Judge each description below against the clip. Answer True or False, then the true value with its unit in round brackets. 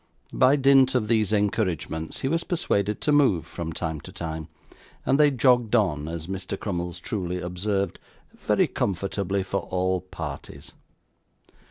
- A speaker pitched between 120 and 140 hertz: False (100 Hz)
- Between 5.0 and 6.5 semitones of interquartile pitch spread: True (5.3 semitones)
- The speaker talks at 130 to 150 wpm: True (145 wpm)